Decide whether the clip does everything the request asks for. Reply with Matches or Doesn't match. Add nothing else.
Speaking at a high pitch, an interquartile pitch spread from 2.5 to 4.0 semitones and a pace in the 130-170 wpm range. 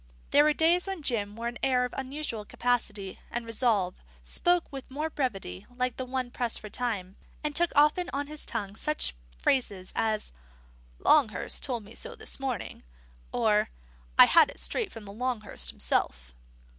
Doesn't match